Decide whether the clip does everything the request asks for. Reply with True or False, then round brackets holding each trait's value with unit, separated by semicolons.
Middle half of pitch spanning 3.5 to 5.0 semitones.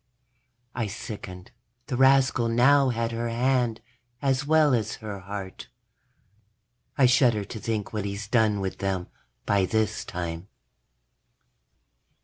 True (4.0 semitones)